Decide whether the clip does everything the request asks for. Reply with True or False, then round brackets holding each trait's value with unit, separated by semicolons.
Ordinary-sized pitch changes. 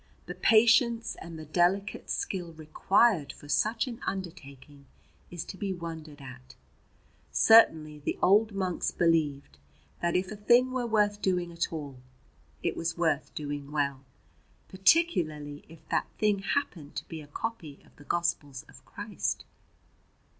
False (5.7 semitones)